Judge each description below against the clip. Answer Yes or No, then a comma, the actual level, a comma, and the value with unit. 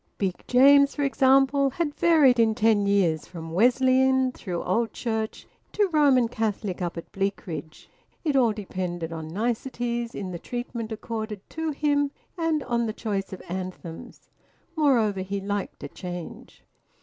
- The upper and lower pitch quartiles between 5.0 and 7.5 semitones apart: Yes, wide, 5.6 semitones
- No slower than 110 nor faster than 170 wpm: Yes, average, 150 wpm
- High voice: Yes, high, 225 Hz